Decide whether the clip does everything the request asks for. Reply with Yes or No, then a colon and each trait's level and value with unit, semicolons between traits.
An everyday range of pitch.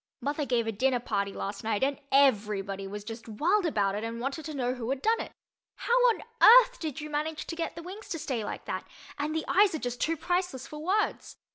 No: wide, 6.6 semitones